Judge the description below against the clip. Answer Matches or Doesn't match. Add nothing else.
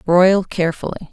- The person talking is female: Matches